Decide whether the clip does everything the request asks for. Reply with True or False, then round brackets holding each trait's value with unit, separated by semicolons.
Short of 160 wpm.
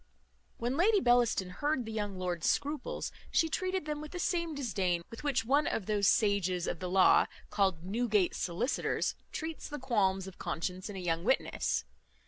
False (175 wpm)